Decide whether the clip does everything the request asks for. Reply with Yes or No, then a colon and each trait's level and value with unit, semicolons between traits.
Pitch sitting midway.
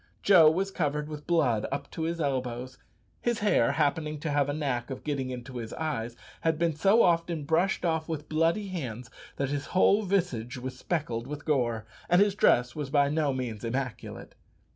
Yes: medium, 150 Hz